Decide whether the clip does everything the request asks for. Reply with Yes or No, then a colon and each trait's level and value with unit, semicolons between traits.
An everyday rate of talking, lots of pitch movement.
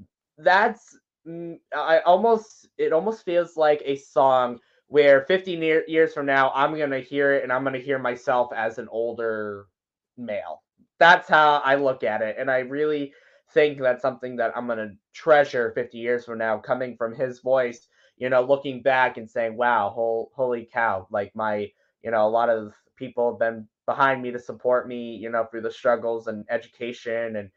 No: average, 190 wpm; average, 3.5 semitones